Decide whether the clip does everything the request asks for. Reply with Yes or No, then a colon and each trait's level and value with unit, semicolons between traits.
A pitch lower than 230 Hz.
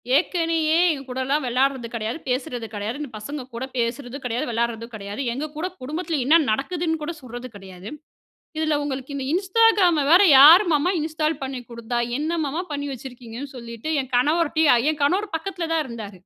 No: very high, 275 Hz